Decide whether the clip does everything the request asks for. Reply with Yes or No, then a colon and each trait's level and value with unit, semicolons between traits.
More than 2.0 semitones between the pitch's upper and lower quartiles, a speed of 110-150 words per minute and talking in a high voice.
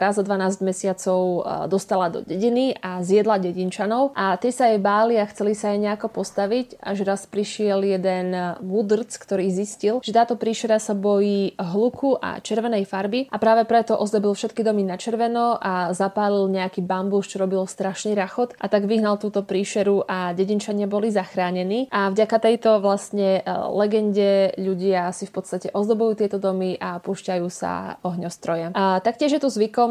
No: narrow, 2.5 semitones; fast, 165 wpm; high, 200 Hz